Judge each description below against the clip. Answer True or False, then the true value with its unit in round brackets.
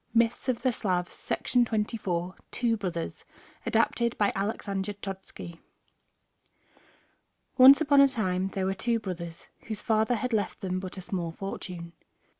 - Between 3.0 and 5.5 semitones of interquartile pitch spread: True (3.9 semitones)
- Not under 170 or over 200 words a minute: False (135 wpm)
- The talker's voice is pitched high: True (200 Hz)